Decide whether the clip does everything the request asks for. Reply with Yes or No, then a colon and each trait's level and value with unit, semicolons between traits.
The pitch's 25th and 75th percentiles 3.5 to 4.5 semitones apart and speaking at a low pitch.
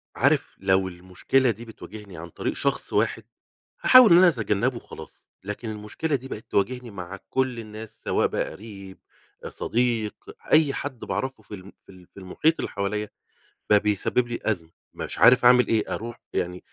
Yes: average, 4.1 semitones; low, 110 Hz